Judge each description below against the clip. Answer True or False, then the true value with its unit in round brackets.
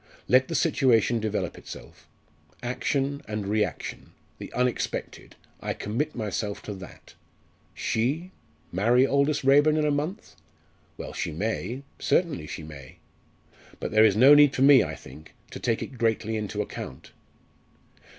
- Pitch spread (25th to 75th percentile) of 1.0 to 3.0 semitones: False (4.9 semitones)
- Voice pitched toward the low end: True (120 Hz)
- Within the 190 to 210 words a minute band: False (140 wpm)